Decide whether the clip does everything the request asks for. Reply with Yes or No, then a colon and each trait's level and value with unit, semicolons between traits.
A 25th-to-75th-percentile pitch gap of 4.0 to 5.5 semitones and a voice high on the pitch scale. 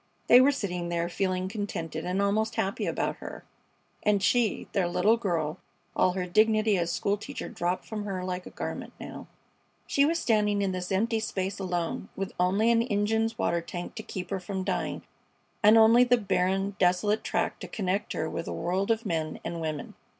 No: average, 3.3 semitones; high, 195 Hz